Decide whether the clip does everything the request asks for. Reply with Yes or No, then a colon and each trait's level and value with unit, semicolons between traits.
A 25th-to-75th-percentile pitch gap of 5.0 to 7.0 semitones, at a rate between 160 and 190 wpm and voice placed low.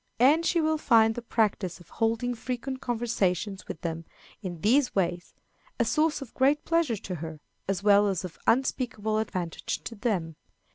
No: wide, 5.5 semitones; average, 170 wpm; high, 220 Hz